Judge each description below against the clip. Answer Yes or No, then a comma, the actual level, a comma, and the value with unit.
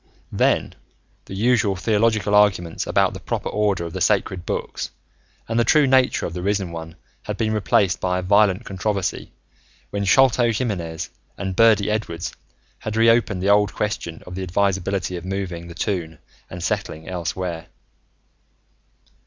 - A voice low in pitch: Yes, very low, 95 Hz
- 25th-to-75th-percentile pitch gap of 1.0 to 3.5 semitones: Yes, average, 3.2 semitones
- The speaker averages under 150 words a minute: No, average, 155 wpm